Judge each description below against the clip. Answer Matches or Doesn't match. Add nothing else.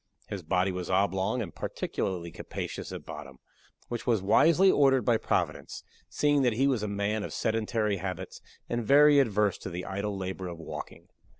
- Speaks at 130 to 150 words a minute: Doesn't match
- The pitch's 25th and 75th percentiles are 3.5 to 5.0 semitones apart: Matches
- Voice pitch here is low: Matches